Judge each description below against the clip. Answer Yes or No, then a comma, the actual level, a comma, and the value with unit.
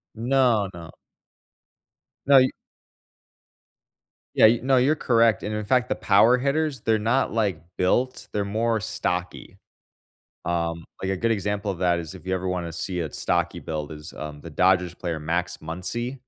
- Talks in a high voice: No, low, 100 Hz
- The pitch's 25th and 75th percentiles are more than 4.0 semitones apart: Yes, average, 5.3 semitones